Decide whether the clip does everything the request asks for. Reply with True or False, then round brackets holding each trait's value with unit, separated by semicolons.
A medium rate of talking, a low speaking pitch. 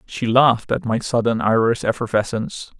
True (150 wpm; 115 Hz)